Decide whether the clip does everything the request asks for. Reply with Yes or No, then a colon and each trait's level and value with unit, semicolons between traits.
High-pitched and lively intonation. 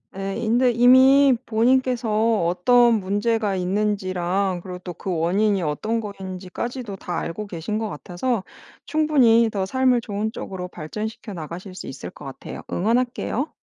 No: high, 210 Hz; average, 4.3 semitones